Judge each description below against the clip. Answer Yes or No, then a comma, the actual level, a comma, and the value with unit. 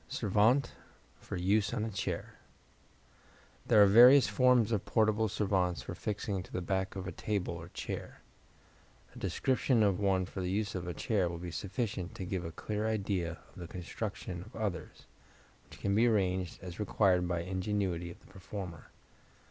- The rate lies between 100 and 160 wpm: No, average, 175 wpm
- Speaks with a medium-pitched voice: No, very low, 95 Hz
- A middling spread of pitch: Yes, average, 3.0 semitones